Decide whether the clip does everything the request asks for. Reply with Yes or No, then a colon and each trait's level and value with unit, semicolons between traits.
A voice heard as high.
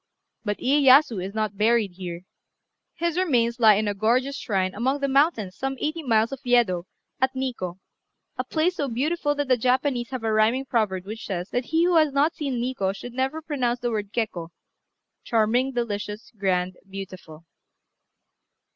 Yes: high, 235 Hz